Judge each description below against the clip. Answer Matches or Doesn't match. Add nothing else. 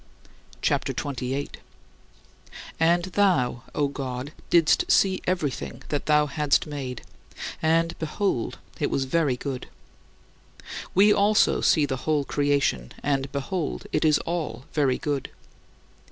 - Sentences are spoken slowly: Matches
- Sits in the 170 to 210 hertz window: Doesn't match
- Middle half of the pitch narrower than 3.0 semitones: Doesn't match